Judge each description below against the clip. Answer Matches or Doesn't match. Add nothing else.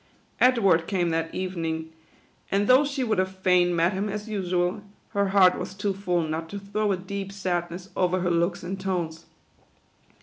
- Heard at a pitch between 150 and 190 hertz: Matches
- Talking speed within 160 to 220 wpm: Matches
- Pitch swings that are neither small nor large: Doesn't match